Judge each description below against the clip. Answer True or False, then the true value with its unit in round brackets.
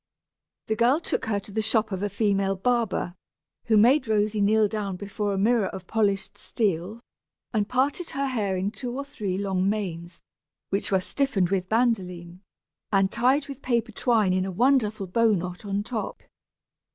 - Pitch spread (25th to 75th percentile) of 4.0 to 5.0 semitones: False (3.4 semitones)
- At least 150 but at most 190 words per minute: True (175 wpm)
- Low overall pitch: False (210 Hz)